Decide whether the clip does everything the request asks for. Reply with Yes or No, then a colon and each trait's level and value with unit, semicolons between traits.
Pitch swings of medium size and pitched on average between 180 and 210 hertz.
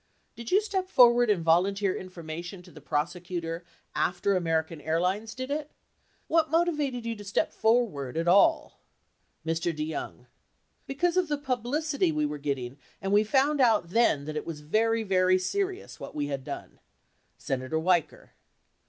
No: wide, 7.6 semitones; high, 190 Hz